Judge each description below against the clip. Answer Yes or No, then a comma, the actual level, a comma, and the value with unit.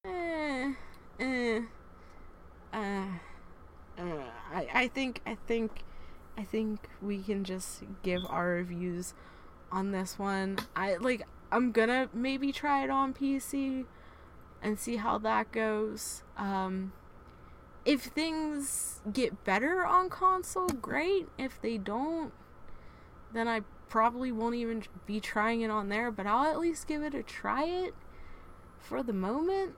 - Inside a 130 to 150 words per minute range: Yes, slow, 135 wpm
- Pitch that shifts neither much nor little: No, wide, 5.9 semitones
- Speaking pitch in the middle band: No, high, 225 Hz